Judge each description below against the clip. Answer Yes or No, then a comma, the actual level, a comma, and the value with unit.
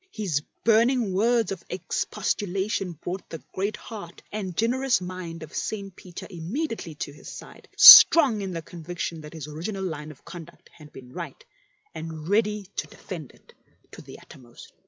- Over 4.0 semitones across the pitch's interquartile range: Yes, average, 4.6 semitones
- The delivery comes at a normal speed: Yes, average, 160 wpm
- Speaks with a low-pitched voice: No, medium, 185 Hz